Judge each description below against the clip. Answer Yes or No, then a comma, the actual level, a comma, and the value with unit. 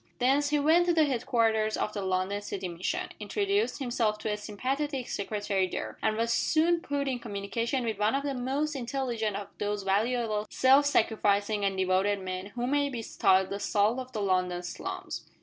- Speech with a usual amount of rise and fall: Yes, average, 5.0 semitones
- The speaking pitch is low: No, high, 220 Hz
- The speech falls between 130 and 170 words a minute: No, average, 185 wpm